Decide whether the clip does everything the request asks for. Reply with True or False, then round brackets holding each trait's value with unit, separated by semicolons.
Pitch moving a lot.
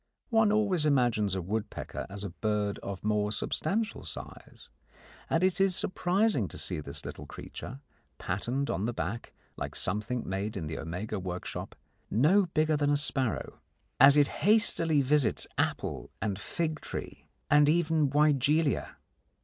True (7.4 semitones)